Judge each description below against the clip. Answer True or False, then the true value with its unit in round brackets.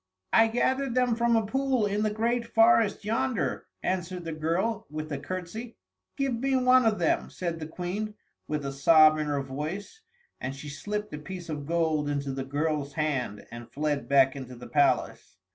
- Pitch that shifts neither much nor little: False (7.5 semitones)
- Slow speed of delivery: False (185 wpm)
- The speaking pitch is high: False (170 Hz)